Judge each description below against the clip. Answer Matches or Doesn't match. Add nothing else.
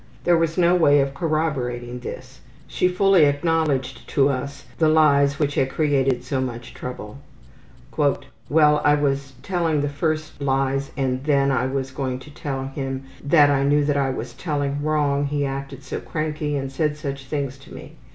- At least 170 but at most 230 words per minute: Matches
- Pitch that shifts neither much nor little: Doesn't match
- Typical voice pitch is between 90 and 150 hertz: Matches